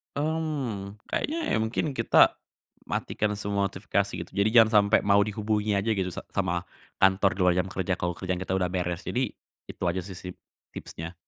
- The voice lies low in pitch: Yes, low, 100 Hz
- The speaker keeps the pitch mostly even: No, average, 3.0 semitones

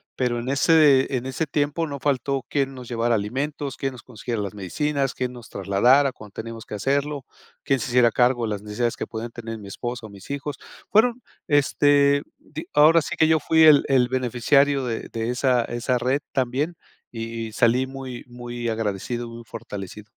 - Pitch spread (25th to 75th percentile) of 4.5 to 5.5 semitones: No, average, 3.4 semitones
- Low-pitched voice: Yes, low, 125 Hz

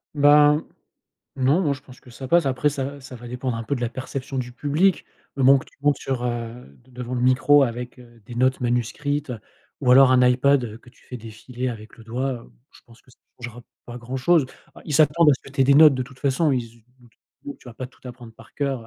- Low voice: Yes, low, 130 Hz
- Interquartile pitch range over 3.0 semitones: No, narrow, 2.5 semitones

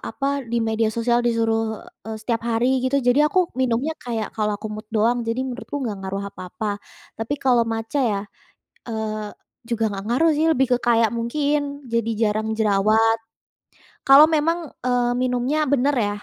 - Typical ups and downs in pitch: Yes, average, 3.0 semitones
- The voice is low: No, high, 235 Hz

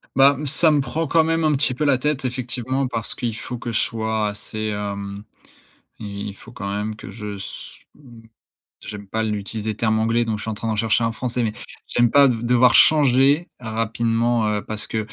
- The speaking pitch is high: No, low, 115 Hz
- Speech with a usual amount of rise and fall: Yes, average, 3.2 semitones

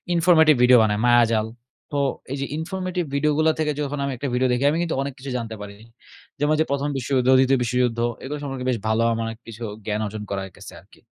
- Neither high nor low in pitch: No, low, 130 Hz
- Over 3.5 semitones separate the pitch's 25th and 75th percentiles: Yes, average, 4.3 semitones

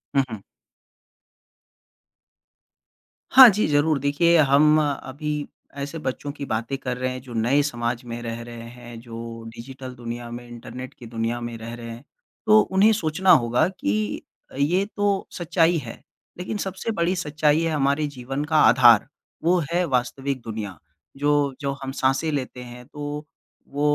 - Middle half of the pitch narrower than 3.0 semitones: No, average, 4.5 semitones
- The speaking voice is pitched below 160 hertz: Yes, low, 135 Hz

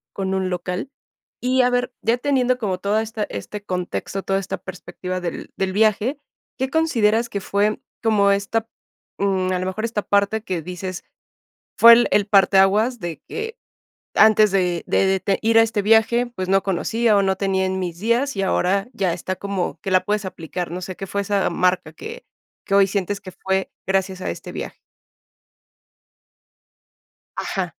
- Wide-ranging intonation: No, average, 3.0 semitones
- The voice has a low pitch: No, high, 200 Hz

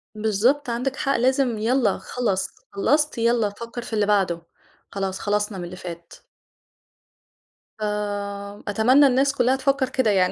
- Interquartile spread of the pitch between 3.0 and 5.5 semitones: Yes, average, 4.2 semitones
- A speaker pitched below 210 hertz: No, high, 220 Hz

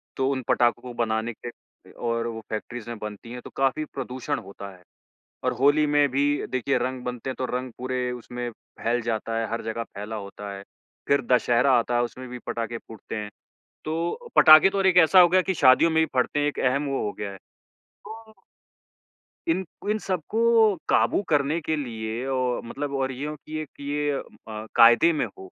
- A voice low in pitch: Yes, low, 130 Hz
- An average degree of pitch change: Yes, average, 4.2 semitones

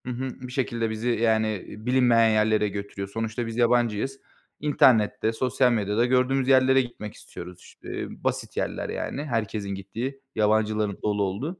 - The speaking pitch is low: Yes, low, 115 Hz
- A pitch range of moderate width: Yes, average, 3.2 semitones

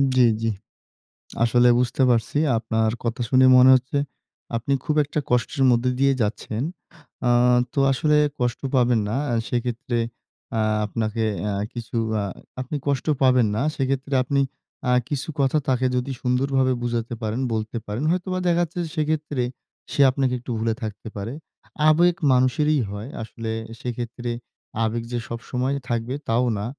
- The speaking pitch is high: No, low, 125 Hz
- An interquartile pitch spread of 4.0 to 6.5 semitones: No, average, 2.9 semitones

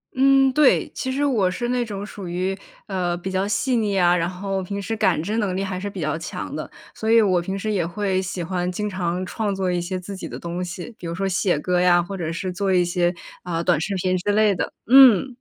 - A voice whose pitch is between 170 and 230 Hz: Yes, high, 190 Hz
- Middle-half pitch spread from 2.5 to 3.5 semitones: Yes, average, 2.8 semitones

